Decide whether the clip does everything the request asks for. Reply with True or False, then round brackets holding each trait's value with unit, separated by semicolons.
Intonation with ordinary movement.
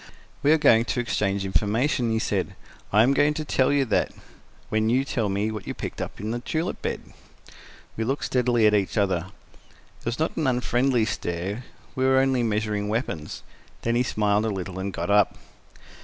True (4.1 semitones)